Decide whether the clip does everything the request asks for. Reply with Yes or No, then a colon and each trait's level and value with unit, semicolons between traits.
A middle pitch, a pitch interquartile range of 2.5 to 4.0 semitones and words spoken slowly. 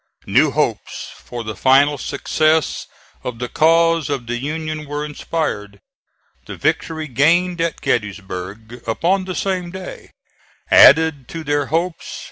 No: medium, 150 Hz; average, 5.3 semitones; slow, 130 wpm